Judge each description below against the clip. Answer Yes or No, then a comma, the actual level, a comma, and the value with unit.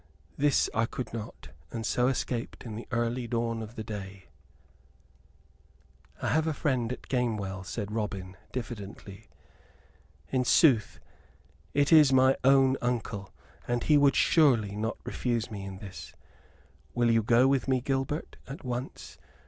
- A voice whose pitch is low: Yes, low, 120 Hz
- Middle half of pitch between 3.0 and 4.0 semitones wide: Yes, average, 3.6 semitones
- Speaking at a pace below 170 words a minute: Yes, average, 150 wpm